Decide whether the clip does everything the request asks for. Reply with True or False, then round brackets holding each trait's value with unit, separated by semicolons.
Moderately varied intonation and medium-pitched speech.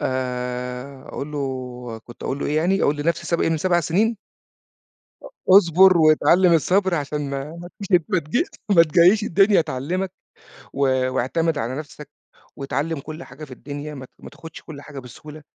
True (4.3 semitones; 150 Hz)